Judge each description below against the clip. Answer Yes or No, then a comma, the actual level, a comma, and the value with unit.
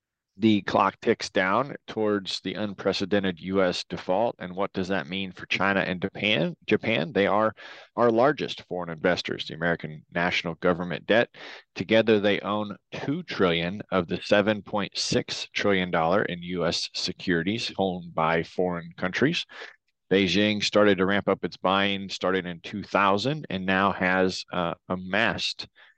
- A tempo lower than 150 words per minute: Yes, average, 140 wpm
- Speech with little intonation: Yes, narrow, 2.2 semitones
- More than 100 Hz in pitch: No, very low, 95 Hz